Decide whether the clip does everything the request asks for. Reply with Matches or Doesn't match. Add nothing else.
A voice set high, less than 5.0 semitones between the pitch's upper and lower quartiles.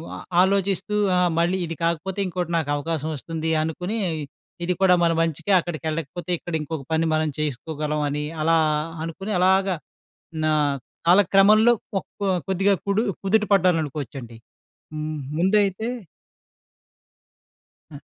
Doesn't match